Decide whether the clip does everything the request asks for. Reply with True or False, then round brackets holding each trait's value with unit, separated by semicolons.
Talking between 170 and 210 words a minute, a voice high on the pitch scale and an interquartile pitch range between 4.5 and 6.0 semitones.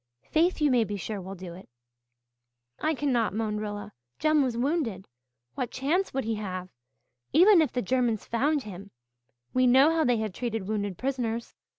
True (175 wpm; 235 Hz; 5.1 semitones)